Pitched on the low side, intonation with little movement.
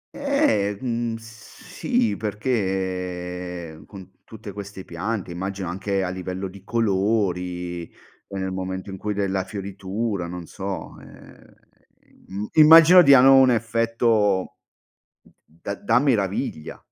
No: low, 100 Hz; average, 3.7 semitones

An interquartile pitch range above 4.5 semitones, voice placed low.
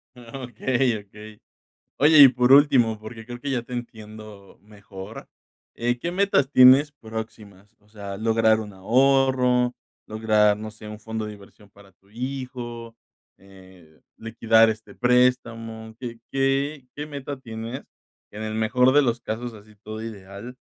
No: average, 2.9 semitones; low, 115 Hz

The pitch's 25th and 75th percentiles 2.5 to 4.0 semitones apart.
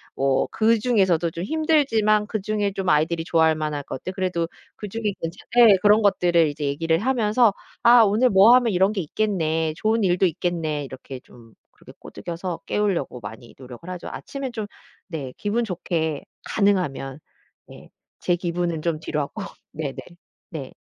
No: average, 5.1 semitones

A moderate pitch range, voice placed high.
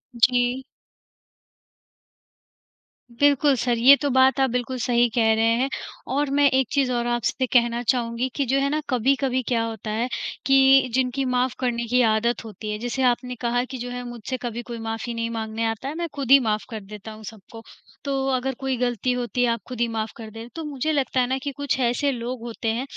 No: narrow, 2.3 semitones; high, 245 Hz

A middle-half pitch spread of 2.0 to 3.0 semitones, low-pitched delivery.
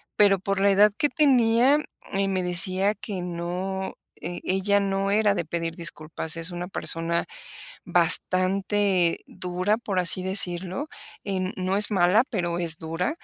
No: narrow, 2.5 semitones; high, 190 Hz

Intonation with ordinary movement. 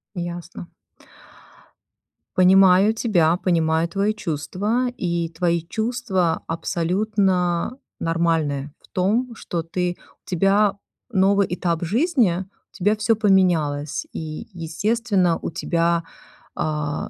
Yes: average, 3.6 semitones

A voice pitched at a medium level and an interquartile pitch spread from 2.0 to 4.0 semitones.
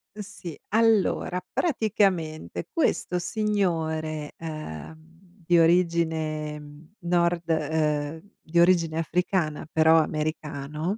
Yes: medium, 165 Hz; narrow, 2.5 semitones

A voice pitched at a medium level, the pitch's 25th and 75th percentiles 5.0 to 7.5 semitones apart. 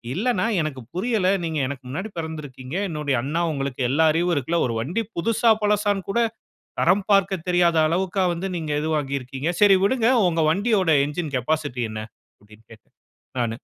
Yes: medium, 165 Hz; wide, 5.6 semitones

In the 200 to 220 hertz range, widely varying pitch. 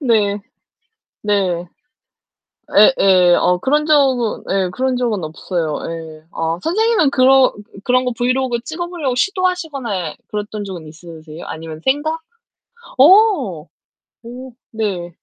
No: high, 230 Hz; wide, 7.3 semitones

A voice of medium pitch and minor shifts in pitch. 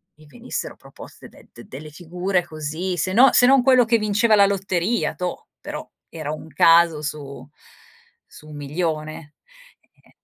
No: medium, 170 Hz; average, 4.6 semitones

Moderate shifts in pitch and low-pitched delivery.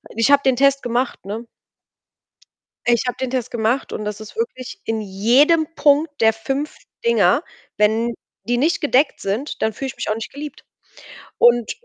No: average, 4.2 semitones; high, 245 Hz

